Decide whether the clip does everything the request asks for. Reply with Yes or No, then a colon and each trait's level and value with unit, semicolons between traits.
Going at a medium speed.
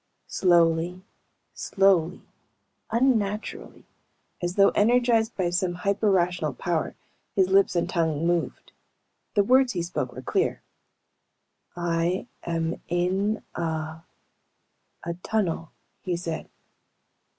No: slow, 105 wpm